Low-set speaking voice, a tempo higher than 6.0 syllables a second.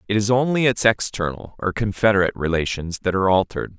Yes: low, 100 Hz; 6.5 syllables/s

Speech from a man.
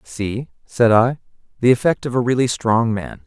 Yes: male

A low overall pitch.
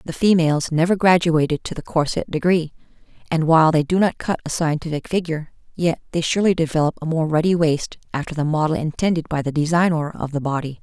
No: medium, 160 Hz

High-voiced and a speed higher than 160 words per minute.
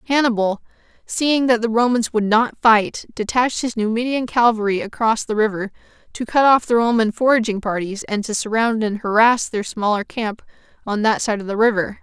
Yes: high, 225 Hz; average, 180 wpm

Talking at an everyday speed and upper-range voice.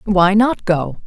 Yes: average, 170 wpm; high, 195 Hz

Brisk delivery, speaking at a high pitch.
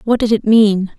Yes: fast, 245 wpm; high, 215 Hz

